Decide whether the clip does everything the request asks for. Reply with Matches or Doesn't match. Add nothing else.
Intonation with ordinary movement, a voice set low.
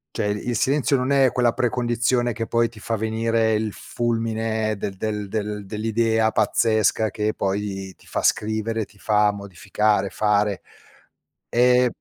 Doesn't match